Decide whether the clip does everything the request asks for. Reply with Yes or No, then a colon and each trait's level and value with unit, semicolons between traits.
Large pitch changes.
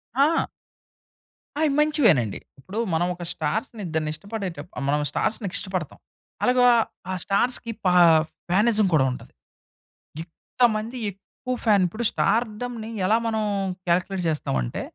Yes: wide, 5.7 semitones